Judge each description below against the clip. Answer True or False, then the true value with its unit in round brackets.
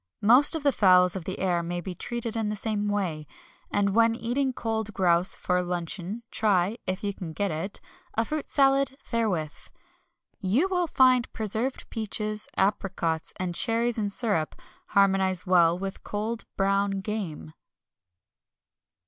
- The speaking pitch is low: False (205 Hz)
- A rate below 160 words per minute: True (150 wpm)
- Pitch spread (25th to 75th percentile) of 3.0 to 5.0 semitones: True (4.0 semitones)